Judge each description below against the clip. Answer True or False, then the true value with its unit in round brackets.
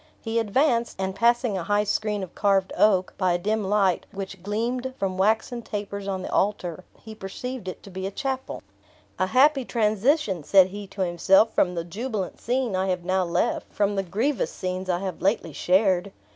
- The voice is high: True (200 Hz)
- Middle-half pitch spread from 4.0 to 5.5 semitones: False (3.1 semitones)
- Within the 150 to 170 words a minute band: False (190 wpm)